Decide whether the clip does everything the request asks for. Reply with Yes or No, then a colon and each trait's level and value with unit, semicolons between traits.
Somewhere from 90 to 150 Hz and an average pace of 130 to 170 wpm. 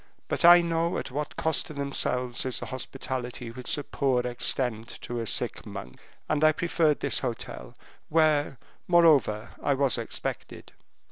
Yes: low, 135 Hz; average, 155 wpm